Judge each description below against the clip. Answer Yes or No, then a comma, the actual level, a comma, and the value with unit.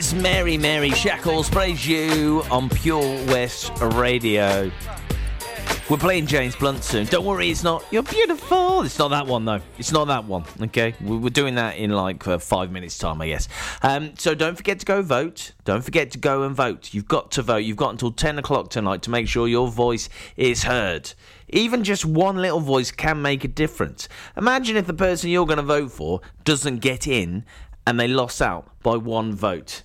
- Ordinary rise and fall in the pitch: No, wide, 6.4 semitones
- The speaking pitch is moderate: No, low, 130 Hz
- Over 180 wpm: Yes, average, 200 wpm